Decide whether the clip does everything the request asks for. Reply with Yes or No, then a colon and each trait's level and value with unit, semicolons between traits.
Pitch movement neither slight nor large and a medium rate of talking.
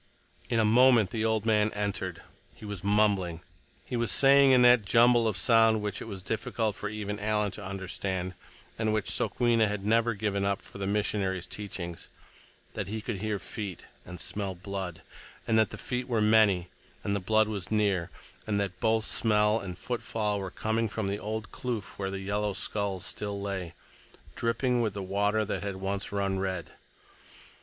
No: narrow, 2.2 semitones; average, 175 wpm